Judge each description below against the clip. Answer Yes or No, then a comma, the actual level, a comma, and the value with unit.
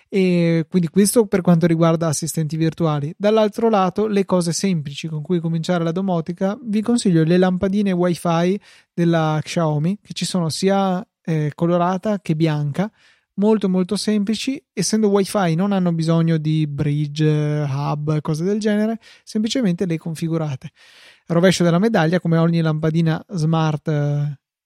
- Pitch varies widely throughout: No, average, 3.6 semitones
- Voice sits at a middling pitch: Yes, medium, 175 Hz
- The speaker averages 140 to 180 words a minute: Yes, average, 145 wpm